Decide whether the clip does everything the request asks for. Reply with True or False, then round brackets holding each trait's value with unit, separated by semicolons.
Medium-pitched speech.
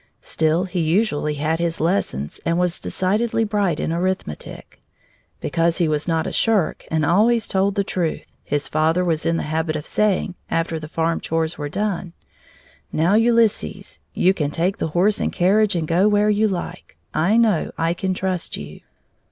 True (175 Hz)